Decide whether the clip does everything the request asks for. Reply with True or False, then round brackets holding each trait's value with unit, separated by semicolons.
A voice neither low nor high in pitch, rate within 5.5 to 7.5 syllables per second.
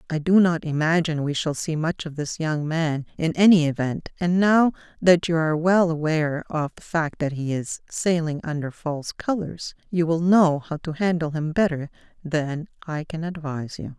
False (160 Hz; 4.9 syllables/s)